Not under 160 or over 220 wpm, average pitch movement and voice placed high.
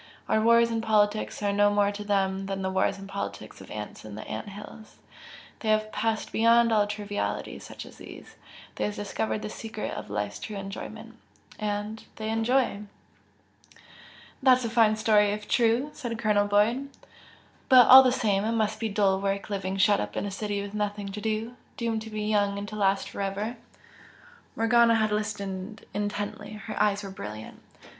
No: average, 180 wpm; narrow, 1.8 semitones; high, 210 Hz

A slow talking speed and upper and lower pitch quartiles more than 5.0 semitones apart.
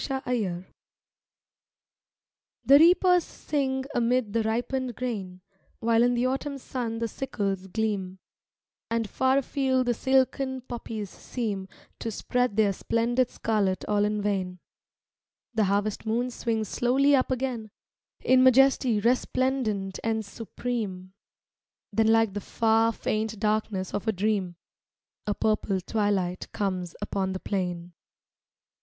No: slow, 125 wpm; average, 3.8 semitones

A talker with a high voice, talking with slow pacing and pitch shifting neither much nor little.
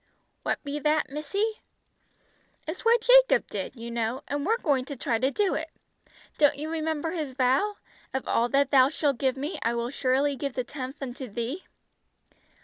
No: very high, 280 Hz; average, 180 wpm; average, 3.5 semitones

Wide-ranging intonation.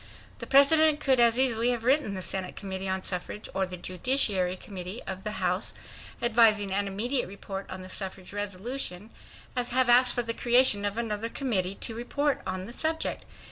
No: average, 4.5 semitones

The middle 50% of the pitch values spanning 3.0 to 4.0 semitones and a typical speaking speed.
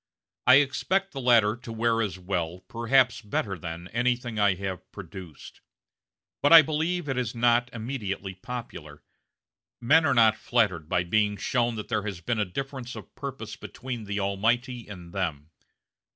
No: average, 4.5 semitones; average, 165 wpm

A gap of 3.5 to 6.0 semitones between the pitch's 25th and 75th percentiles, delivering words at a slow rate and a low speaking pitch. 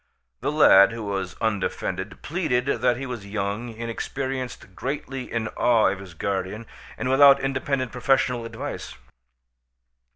Yes: average, 4.8 semitones; slow, 130 wpm; low, 115 Hz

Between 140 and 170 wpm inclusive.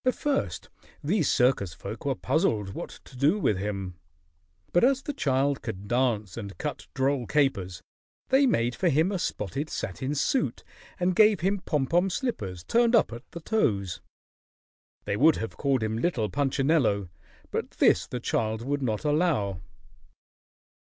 Yes: average, 160 wpm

